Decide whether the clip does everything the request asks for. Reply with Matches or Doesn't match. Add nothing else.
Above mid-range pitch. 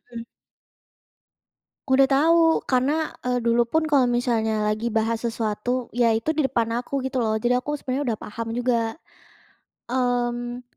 Matches